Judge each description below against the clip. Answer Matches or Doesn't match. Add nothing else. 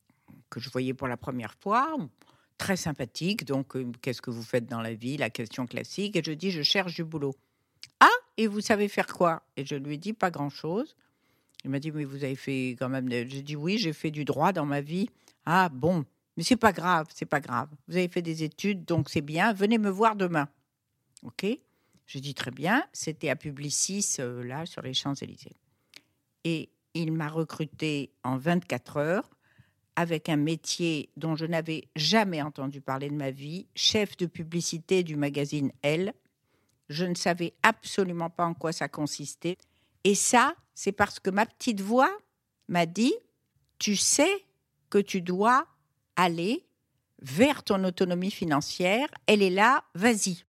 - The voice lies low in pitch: Doesn't match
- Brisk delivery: Doesn't match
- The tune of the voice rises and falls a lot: Matches